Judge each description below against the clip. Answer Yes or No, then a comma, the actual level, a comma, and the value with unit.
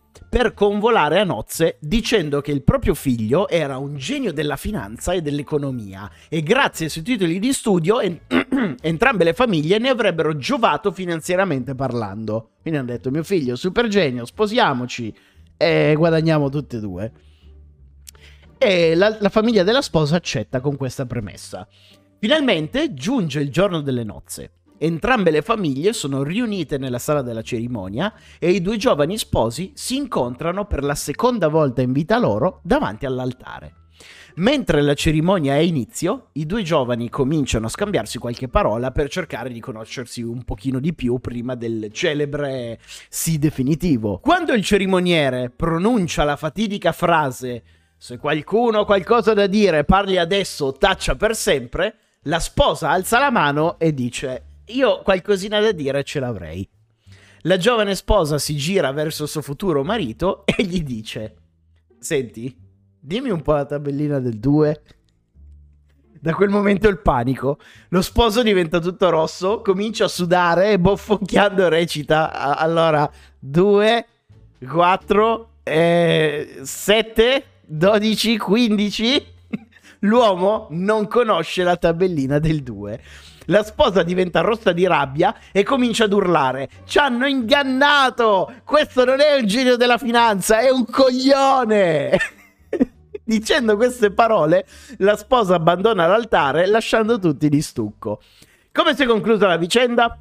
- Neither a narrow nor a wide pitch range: No, wide, 8.0 semitones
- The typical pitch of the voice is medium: Yes, medium, 165 Hz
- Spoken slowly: No, average, 140 wpm